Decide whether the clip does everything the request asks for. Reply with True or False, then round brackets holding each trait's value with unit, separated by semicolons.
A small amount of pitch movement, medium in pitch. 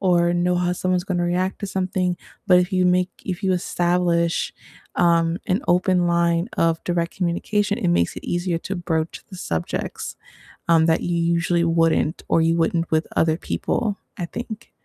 True (1.4 semitones; 175 Hz)